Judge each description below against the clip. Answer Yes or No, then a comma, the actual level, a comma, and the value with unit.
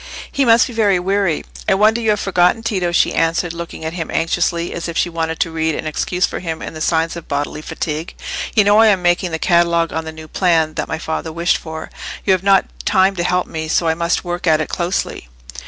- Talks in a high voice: No, medium, 170 Hz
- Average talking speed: No, fast, 240 wpm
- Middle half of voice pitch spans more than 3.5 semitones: No, average, 2.7 semitones